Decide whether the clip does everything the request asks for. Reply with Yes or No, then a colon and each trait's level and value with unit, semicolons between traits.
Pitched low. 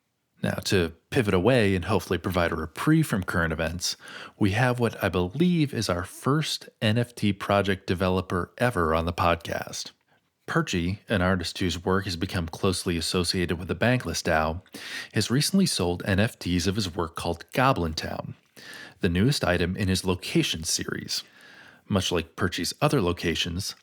Yes: very low, 95 Hz